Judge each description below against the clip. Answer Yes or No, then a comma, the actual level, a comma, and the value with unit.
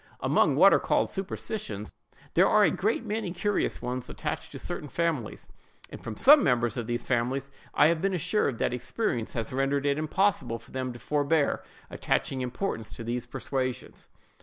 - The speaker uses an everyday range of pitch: No, wide, 7.2 semitones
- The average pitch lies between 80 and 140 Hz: Yes, low, 135 Hz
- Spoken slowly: No, average, 175 wpm